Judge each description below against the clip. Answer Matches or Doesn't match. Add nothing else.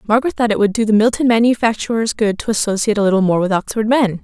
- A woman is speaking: Matches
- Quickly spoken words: Matches